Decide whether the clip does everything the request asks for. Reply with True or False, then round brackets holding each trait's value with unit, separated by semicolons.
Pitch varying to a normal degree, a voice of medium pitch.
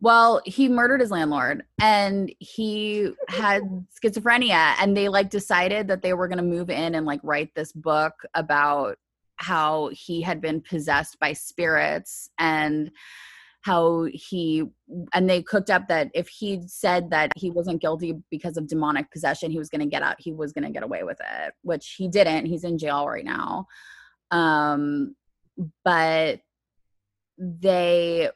True (3.5 semitones; 170 Hz)